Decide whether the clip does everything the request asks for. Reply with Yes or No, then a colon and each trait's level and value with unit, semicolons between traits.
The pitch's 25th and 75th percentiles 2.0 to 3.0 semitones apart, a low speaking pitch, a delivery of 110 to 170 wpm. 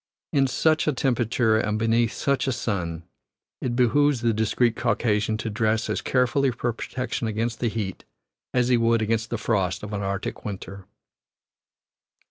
Yes: average, 2.7 semitones; low, 115 Hz; average, 160 wpm